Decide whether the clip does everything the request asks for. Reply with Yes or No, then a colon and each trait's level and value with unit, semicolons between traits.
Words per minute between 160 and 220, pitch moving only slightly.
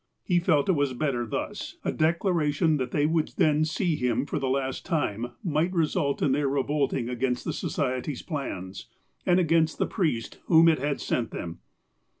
No: average, 175 wpm; average, 3.9 semitones